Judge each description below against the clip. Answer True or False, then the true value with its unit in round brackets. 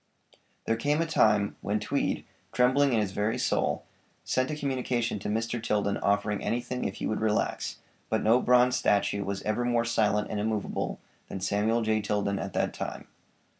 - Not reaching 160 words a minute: False (175 wpm)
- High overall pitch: False (110 Hz)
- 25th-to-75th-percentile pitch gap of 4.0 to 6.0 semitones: False (3.0 semitones)